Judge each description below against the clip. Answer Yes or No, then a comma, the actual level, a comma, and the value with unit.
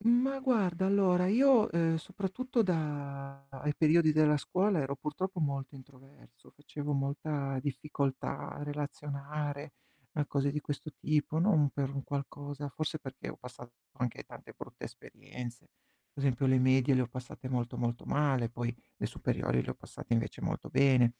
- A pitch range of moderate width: Yes, average, 3.0 semitones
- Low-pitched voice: No, medium, 145 Hz